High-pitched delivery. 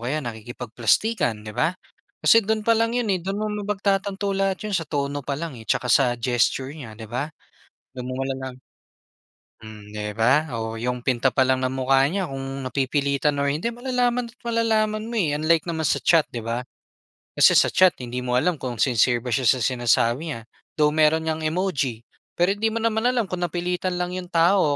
No: medium, 150 Hz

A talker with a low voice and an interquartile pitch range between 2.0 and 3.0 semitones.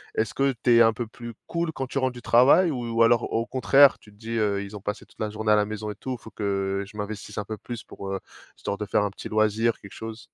Yes: low, 110 Hz; narrow, 2.6 semitones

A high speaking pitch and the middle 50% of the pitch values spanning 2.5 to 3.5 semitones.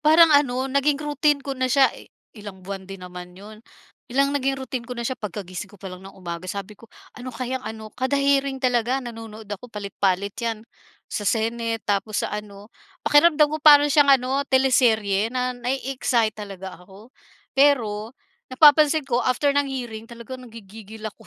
No: high, 235 Hz; average, 4.5 semitones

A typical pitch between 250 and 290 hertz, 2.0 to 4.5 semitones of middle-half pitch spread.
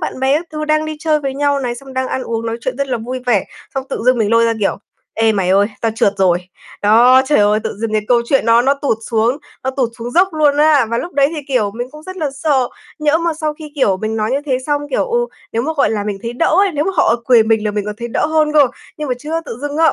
No: very high, 260 Hz; average, 4.9 semitones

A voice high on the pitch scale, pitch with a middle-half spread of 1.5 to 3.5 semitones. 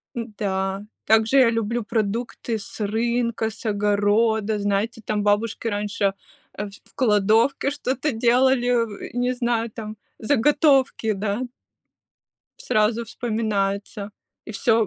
Yes: high, 220 Hz; narrow, 2.4 semitones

